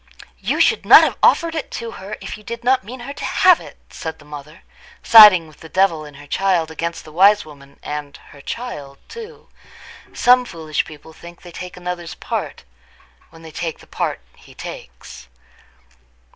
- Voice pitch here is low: No, medium, 170 Hz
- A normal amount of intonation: No, wide, 6.7 semitones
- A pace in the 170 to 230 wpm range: Yes, average, 185 wpm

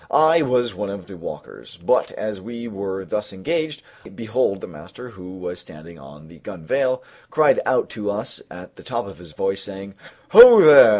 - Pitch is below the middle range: Yes, low, 100 Hz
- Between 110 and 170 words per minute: No, average, 185 wpm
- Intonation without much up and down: No, average, 5.0 semitones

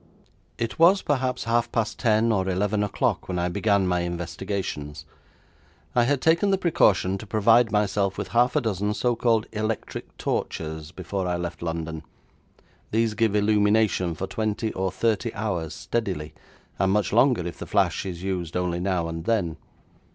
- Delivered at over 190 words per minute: No, average, 165 wpm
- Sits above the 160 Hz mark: No, low, 100 Hz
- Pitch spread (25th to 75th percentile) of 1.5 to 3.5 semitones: No, average, 4.3 semitones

